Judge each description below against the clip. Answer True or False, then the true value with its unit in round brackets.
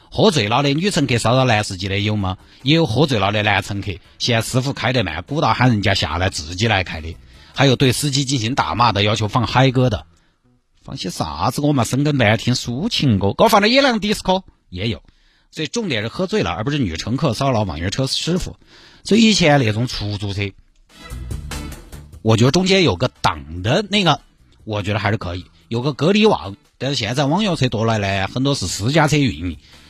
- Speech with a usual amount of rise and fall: False (6.3 semitones)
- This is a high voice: False (120 Hz)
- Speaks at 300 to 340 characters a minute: True (315 characters per minute)